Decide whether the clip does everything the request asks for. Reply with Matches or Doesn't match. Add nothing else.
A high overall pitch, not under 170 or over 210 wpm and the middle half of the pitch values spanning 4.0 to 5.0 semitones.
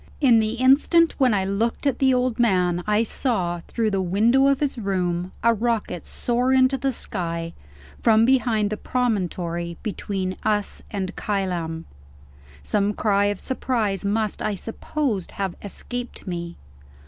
Doesn't match